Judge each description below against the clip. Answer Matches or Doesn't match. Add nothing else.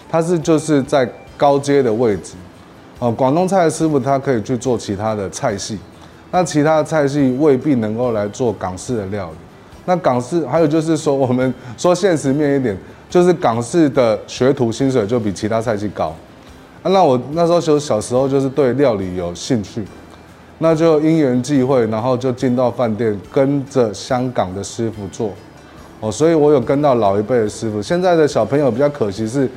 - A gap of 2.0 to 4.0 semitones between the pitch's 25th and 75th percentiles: Doesn't match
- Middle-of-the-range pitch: Doesn't match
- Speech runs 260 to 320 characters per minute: Matches